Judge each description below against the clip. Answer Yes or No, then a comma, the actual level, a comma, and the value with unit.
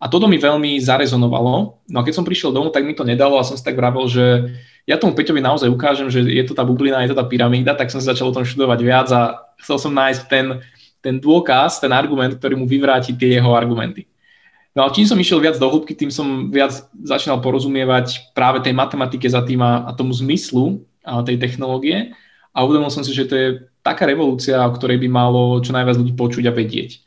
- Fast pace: Yes, fast, 225 wpm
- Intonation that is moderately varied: No, narrow, 1.9 semitones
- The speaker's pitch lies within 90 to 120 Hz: No, low, 130 Hz